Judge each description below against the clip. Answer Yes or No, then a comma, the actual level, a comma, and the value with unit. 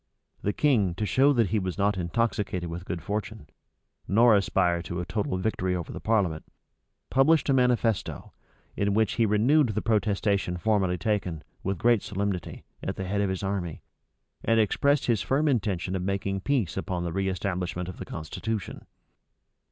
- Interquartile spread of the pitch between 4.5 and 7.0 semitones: No, average, 3.6 semitones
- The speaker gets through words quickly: No, average, 165 wpm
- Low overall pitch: Yes, low, 100 Hz